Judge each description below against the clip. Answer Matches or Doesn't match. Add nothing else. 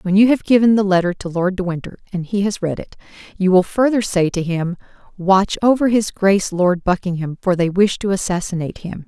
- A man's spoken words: Doesn't match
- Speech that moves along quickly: Matches